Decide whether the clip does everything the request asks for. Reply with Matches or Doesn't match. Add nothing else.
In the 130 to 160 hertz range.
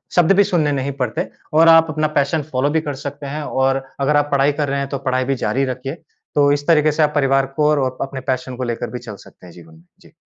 Matches